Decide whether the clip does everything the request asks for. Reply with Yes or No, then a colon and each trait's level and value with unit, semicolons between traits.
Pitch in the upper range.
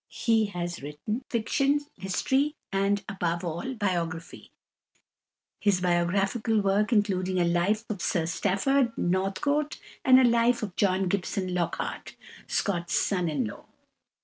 Yes: high, 195 Hz